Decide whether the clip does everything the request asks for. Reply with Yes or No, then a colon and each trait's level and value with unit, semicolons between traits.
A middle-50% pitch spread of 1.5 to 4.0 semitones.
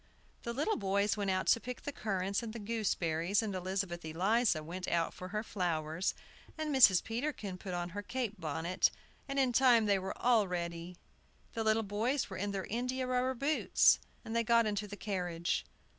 No: average, 4.4 semitones